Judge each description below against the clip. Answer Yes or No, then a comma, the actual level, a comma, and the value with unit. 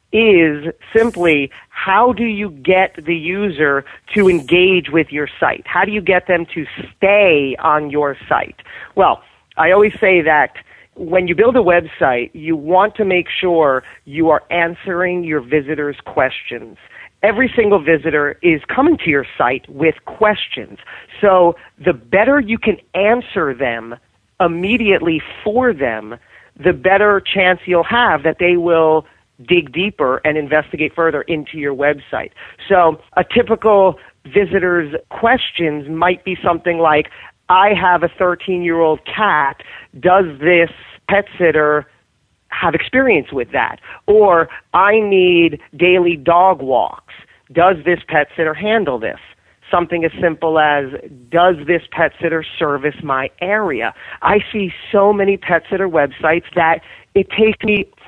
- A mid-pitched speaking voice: Yes, medium, 175 Hz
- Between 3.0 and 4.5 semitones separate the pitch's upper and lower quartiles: Yes, average, 4.1 semitones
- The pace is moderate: Yes, average, 145 wpm